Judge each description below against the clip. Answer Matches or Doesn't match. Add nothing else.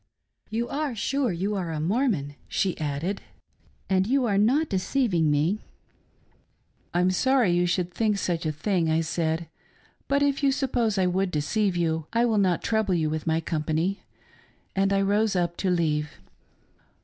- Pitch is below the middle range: Doesn't match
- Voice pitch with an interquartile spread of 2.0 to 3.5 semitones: Doesn't match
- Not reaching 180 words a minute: Doesn't match